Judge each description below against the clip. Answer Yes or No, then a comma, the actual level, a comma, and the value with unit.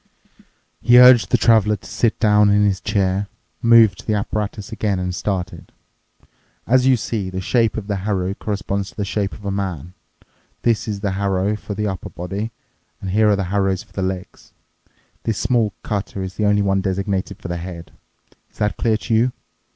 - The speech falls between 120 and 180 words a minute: No, average, 195 wpm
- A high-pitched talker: No, low, 100 Hz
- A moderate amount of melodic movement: No, narrow, 2.2 semitones